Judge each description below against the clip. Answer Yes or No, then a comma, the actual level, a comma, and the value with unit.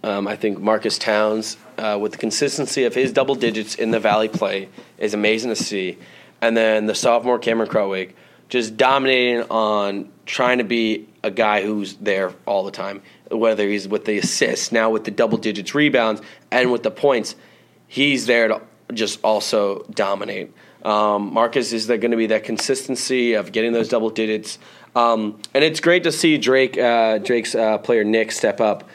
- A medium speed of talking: Yes, average, 185 wpm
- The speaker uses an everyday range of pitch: No, narrow, 2.2 semitones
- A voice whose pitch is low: Yes, low, 110 Hz